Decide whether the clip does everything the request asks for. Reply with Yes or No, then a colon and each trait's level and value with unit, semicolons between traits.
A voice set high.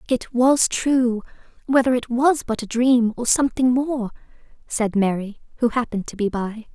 Yes: high, 240 Hz